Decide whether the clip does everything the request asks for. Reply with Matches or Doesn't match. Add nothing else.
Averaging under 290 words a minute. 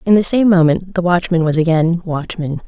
Matches